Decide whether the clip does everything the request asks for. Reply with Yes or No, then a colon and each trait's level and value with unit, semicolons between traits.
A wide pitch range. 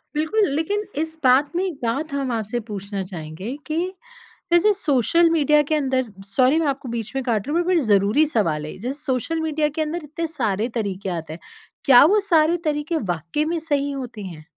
Yes: wide, 6.6 semitones